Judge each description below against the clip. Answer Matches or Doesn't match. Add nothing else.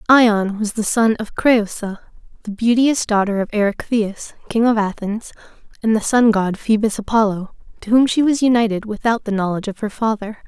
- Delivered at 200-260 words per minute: Doesn't match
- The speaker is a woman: Matches